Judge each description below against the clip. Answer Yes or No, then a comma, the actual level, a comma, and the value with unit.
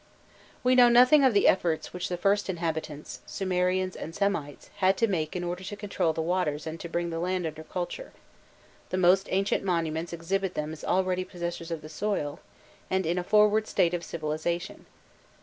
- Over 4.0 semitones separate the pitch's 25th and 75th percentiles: No, average, 2.9 semitones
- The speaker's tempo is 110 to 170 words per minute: No, average, 185 wpm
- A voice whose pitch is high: No, medium, 180 Hz